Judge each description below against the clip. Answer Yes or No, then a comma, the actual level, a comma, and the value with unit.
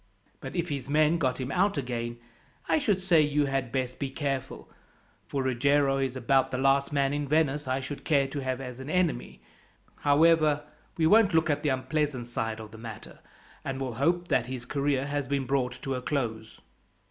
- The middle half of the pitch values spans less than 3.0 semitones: Yes, narrow, 2.4 semitones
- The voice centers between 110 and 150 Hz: Yes, low, 135 Hz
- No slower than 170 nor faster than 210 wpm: Yes, average, 195 wpm